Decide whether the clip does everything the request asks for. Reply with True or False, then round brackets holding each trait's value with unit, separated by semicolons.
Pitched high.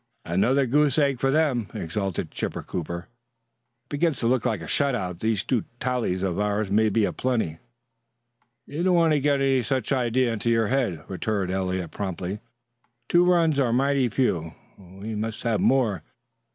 False (115 Hz)